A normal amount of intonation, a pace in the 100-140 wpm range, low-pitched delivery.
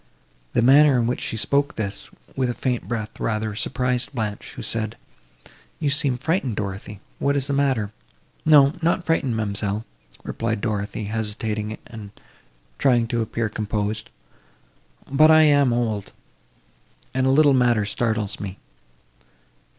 Yes: average, 4.2 semitones; slow, 135 wpm; low, 115 Hz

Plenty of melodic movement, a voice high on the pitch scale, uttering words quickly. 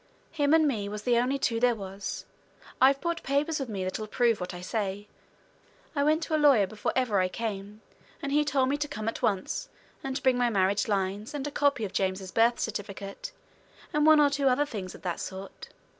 Yes: wide, 6.0 semitones; high, 230 Hz; fast, 220 wpm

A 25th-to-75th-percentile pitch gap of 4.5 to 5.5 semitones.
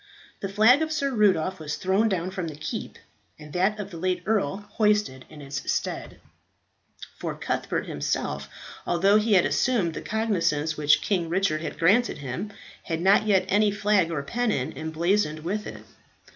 Yes: average, 4.9 semitones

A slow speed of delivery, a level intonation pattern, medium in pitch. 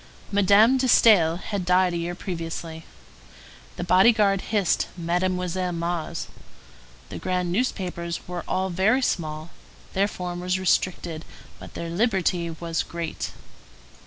Yes: slow, 130 wpm; narrow, 2.3 semitones; medium, 180 Hz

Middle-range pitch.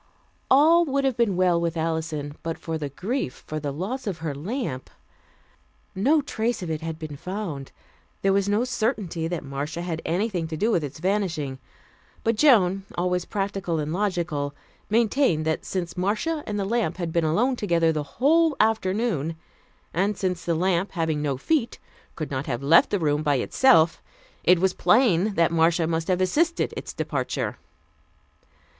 Yes: medium, 180 Hz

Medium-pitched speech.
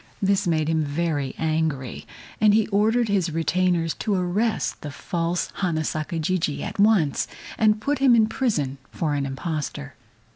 Yes: medium, 170 Hz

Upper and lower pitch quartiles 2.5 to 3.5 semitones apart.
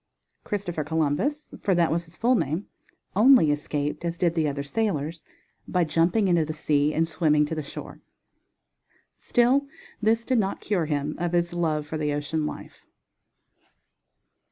No: average, 4.2 semitones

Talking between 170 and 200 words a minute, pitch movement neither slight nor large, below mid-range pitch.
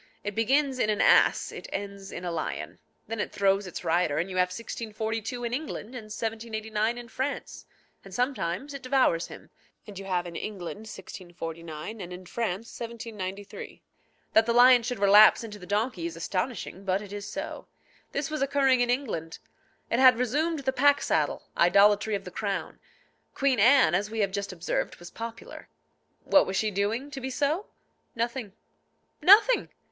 No: average, 175 wpm; average, 4.5 semitones; high, 215 Hz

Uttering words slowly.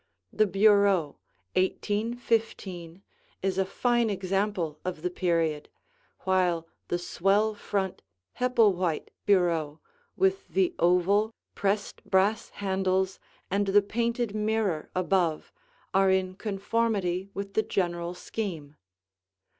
Yes: slow, 105 wpm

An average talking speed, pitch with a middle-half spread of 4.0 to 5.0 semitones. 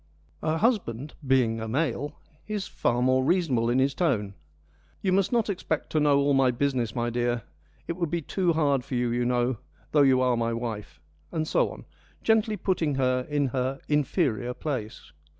Yes: average, 185 wpm; average, 4.7 semitones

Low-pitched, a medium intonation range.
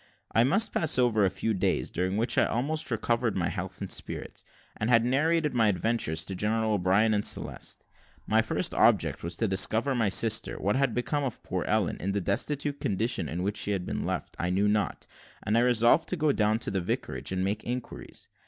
Yes: low, 110 Hz; average, 4.0 semitones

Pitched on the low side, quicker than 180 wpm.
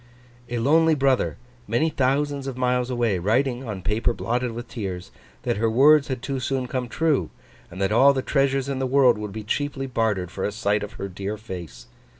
Yes: low, 120 Hz; average, 200 wpm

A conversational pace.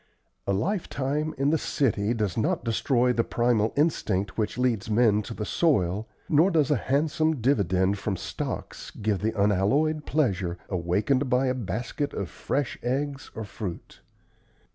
Yes: average, 150 wpm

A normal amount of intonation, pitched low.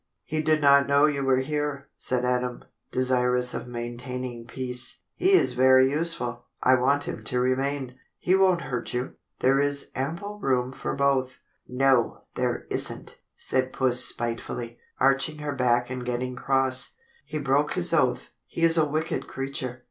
No: narrow, 2.2 semitones; low, 130 Hz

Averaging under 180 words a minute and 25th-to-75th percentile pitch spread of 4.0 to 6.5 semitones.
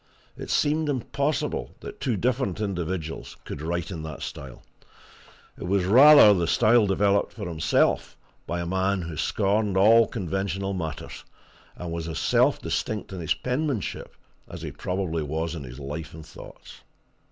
Yes: average, 155 wpm; average, 4.5 semitones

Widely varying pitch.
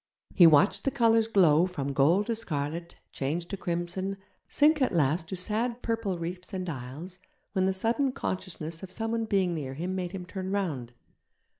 No: average, 4.2 semitones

